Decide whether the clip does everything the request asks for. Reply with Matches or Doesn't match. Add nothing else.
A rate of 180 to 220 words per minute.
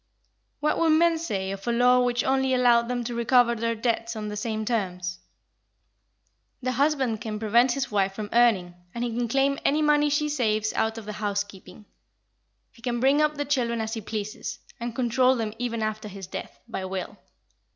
Matches